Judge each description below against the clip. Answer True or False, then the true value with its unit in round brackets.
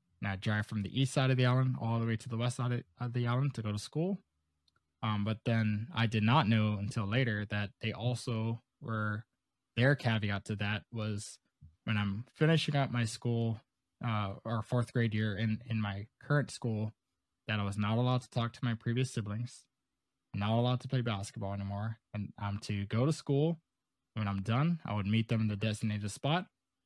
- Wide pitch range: False (2.9 semitones)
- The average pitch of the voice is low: True (115 Hz)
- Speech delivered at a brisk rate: True (210 wpm)